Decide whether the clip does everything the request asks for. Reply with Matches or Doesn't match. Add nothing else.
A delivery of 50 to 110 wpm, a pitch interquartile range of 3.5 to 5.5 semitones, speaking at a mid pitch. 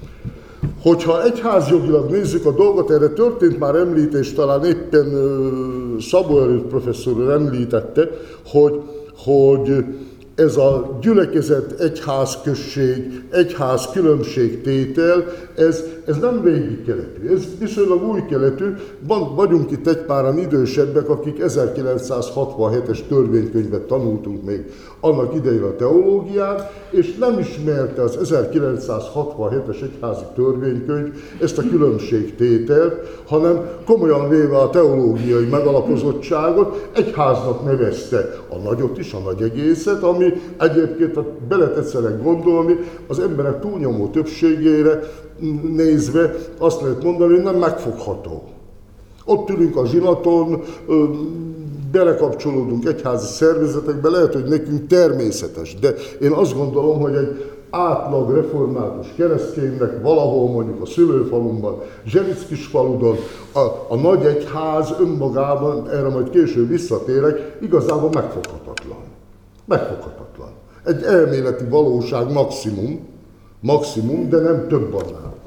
Matches